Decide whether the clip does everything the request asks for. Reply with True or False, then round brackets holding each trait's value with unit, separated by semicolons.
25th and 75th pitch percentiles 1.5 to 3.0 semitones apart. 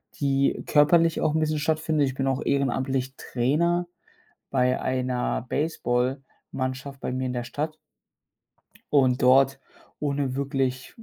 True (2.5 semitones)